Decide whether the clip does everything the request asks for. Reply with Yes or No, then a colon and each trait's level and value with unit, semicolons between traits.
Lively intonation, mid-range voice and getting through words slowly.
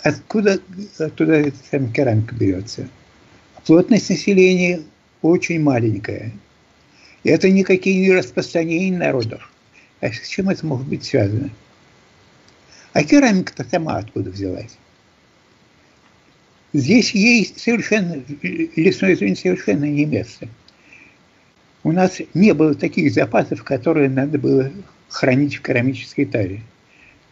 Yes: wide, 7.0 semitones; medium, 150 Hz; slow, 105 wpm